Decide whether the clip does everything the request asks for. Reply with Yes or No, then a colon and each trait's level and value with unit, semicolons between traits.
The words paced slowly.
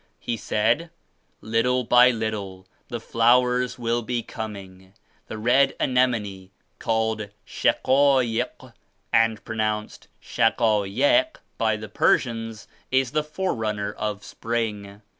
Yes: slow, 105 wpm